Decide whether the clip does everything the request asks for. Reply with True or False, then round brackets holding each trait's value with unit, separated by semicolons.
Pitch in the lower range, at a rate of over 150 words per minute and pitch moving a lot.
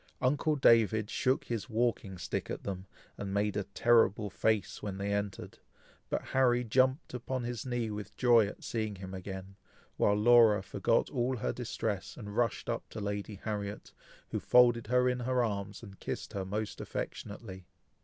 False (110 Hz; 170 wpm; 3.2 semitones)